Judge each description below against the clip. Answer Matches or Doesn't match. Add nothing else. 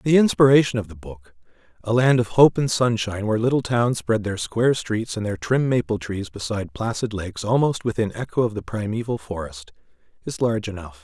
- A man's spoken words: Matches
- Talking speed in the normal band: Matches